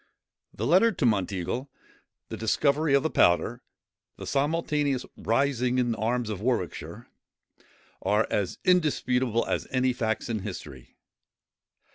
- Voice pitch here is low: Yes, low, 125 Hz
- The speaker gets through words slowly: Yes, slow, 115 wpm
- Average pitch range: Yes, average, 4.3 semitones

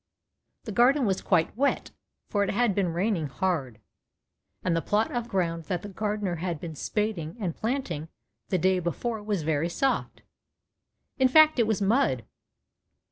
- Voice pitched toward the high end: Yes, high, 195 Hz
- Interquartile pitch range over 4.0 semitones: Yes, average, 4.9 semitones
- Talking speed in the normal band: Yes, average, 160 wpm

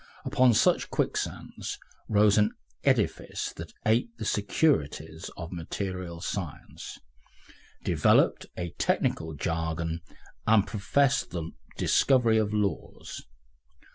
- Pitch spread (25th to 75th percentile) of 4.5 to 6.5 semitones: Yes, average, 4.9 semitones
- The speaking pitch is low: Yes, low, 100 Hz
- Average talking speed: No, slow, 100 wpm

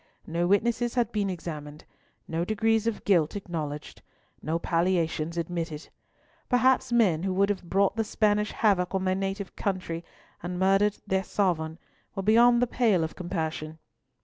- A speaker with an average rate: Yes, average, 155 wpm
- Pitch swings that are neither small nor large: Yes, average, 4.0 semitones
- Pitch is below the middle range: No, high, 190 Hz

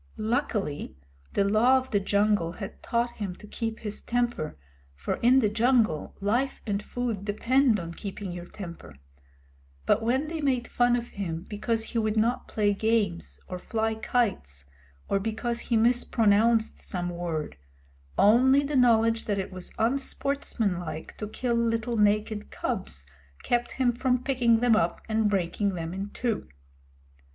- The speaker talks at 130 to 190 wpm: Yes, average, 155 wpm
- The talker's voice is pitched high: Yes, high, 220 Hz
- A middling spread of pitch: Yes, average, 3.3 semitones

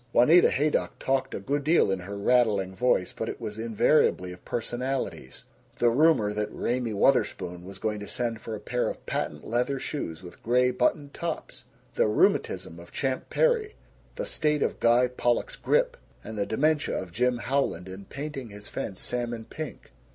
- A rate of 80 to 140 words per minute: No, average, 175 wpm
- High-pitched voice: No, low, 120 Hz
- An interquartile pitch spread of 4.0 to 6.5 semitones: Yes, wide, 5.4 semitones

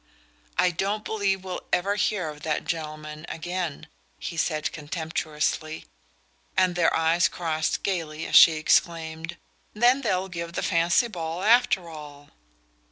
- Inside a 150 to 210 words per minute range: No, slow, 135 wpm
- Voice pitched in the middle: Yes, medium, 170 Hz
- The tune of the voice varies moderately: Yes, average, 3.0 semitones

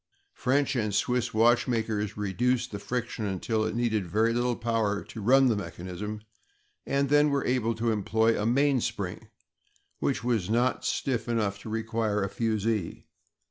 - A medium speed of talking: Yes, average, 150 wpm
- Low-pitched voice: Yes, low, 115 Hz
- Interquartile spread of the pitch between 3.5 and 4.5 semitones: No, narrow, 2.6 semitones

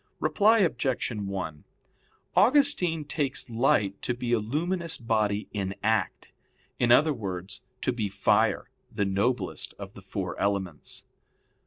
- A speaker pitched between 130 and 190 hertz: No, low, 120 Hz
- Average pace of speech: No, slow, 130 wpm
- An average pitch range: No, wide, 6.9 semitones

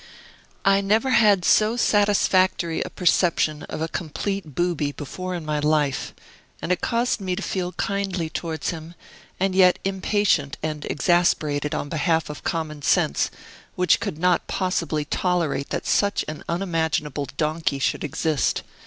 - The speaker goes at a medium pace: Yes, average, 145 wpm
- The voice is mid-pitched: Yes, medium, 170 Hz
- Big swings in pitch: No, average, 3.9 semitones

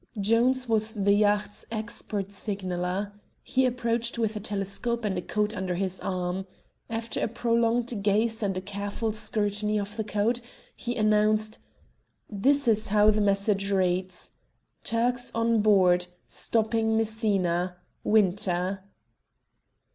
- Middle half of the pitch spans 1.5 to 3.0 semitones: Yes, narrow, 2.5 semitones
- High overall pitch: Yes, high, 210 Hz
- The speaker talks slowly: Yes, slow, 125 wpm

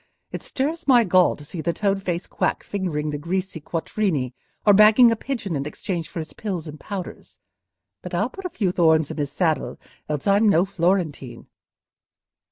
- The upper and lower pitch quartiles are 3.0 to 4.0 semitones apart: No, average, 4.7 semitones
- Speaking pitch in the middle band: Yes, medium, 180 Hz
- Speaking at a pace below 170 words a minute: No, average, 180 wpm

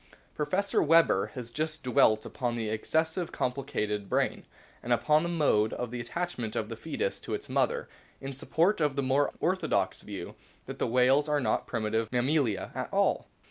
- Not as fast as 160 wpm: No, average, 180 wpm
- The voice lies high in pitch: No, low, 135 Hz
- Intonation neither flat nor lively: No, wide, 5.9 semitones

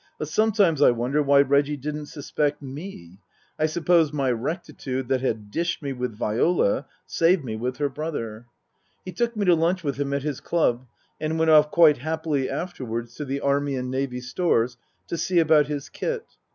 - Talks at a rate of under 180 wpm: No, average, 185 wpm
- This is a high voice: No, medium, 145 Hz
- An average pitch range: Yes, average, 4.0 semitones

